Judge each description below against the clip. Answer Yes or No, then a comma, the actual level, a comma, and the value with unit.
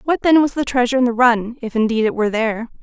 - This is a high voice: Yes, high, 240 Hz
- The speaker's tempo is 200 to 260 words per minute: No, fast, 275 wpm